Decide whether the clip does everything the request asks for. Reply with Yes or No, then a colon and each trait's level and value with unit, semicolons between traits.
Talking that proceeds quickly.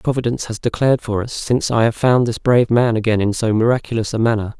Yes: fast, 235 wpm